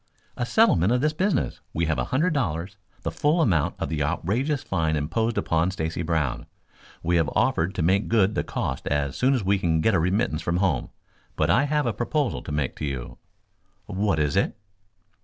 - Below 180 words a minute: No, average, 200 wpm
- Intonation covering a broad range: Yes, wide, 7.1 semitones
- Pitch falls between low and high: No, very low, 95 Hz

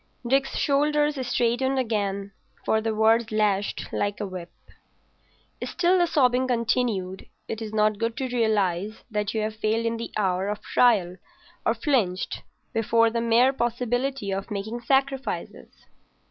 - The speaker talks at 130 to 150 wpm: Yes, average, 145 wpm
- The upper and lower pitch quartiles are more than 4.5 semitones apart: No, average, 3.2 semitones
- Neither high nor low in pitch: No, high, 230 Hz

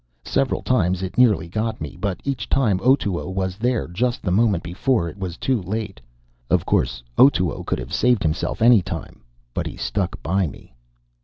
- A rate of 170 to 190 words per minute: Yes, average, 180 wpm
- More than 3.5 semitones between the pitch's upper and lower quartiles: Yes, average, 5.0 semitones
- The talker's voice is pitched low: Yes, low, 100 Hz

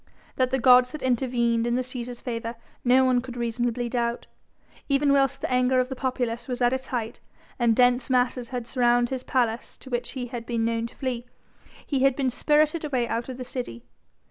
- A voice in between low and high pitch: No, very high, 250 Hz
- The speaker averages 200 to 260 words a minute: Yes, fast, 205 wpm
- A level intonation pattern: Yes, narrow, 1.6 semitones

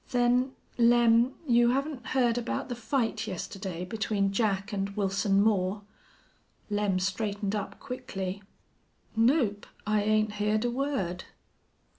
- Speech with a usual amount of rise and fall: Yes, average, 3.5 semitones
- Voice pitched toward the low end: No, high, 215 Hz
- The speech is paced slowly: Yes, slow, 120 wpm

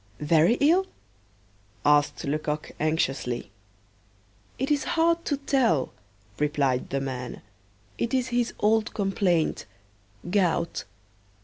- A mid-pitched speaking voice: Yes, medium, 175 Hz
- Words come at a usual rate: No, slow, 100 wpm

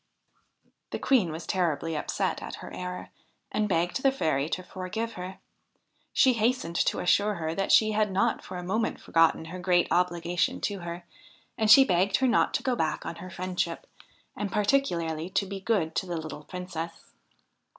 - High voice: No, medium, 180 Hz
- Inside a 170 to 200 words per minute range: Yes, average, 180 wpm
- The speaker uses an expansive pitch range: No, average, 3.7 semitones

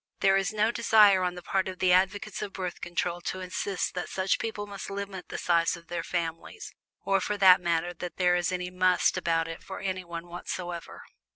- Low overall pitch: No, medium, 185 Hz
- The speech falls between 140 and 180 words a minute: No, fast, 205 wpm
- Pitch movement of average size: No, narrow, 1.8 semitones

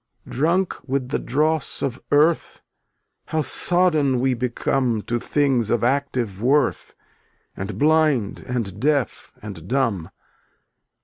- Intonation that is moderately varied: Yes, average, 4.1 semitones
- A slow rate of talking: Yes, slow, 120 wpm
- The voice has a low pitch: Yes, low, 130 Hz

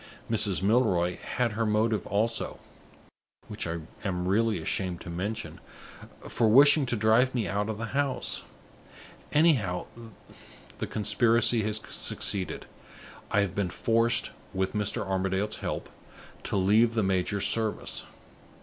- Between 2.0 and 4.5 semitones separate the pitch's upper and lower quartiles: Yes, average, 3.2 semitones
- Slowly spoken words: Yes, slow, 130 wpm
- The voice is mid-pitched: No, low, 105 Hz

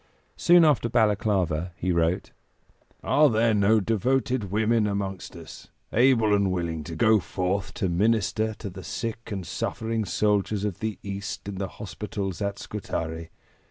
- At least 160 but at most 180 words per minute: No, average, 150 wpm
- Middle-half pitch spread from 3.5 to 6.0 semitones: No, average, 2.9 semitones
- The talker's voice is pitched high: No, low, 105 Hz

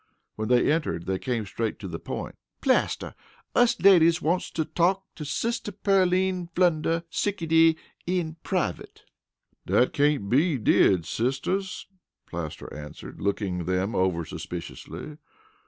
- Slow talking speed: Yes, slow, 125 wpm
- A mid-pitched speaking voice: Yes, medium, 155 Hz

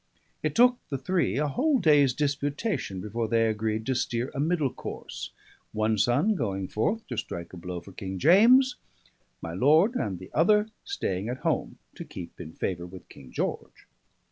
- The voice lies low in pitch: Yes, low, 125 Hz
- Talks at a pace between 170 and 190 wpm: Yes, average, 175 wpm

